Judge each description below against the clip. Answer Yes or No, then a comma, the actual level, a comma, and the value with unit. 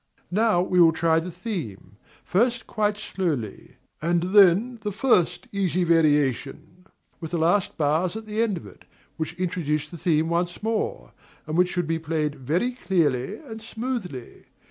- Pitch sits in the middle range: Yes, medium, 175 Hz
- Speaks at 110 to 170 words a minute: Yes, average, 160 wpm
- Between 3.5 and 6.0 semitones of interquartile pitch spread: Yes, average, 4.6 semitones